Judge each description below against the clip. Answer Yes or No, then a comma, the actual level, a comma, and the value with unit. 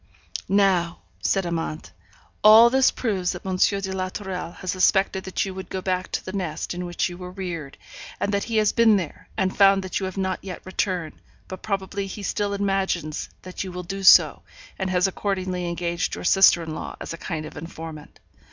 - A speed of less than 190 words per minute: No, fast, 205 wpm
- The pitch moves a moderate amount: No, narrow, 1.9 semitones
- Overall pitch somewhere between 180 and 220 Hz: Yes, medium, 185 Hz